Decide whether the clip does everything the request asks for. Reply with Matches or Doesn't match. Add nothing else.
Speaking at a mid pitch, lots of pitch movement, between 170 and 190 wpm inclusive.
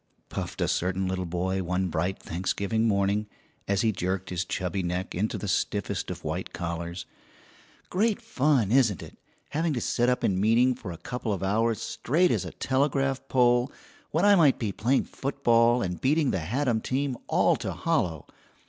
Doesn't match